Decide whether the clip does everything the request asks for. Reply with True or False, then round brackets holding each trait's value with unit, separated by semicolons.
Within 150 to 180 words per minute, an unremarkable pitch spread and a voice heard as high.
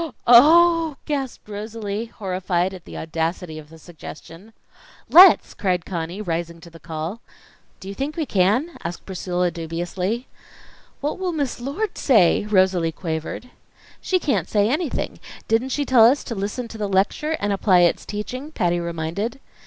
False (155 wpm; 6.6 semitones; 200 Hz)